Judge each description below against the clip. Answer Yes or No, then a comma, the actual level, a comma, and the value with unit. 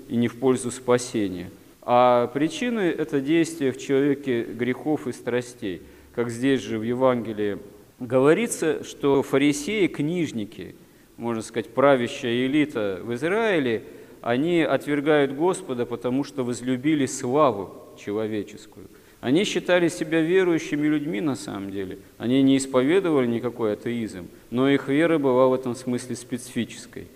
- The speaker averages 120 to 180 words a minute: Yes, average, 130 wpm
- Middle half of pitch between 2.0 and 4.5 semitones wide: Yes, average, 3.2 semitones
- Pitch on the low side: Yes, low, 125 Hz